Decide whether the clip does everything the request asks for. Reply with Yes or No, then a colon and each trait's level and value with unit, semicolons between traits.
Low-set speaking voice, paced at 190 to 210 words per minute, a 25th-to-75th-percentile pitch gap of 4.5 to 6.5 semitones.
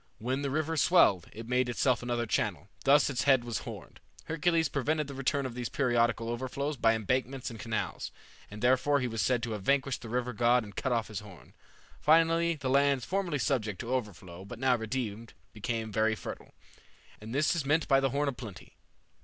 No: low, 125 Hz; average, 200 wpm; average, 3.7 semitones